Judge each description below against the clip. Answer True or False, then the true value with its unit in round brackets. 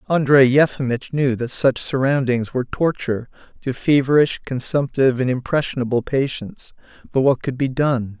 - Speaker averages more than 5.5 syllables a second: False (5.1 syllables/s)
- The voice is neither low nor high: False (130 Hz)